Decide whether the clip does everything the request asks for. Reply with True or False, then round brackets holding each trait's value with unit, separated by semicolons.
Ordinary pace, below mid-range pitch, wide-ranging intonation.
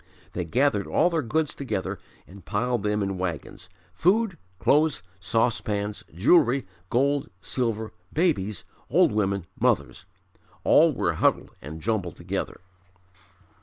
False (120 wpm; 110 Hz; 6.4 semitones)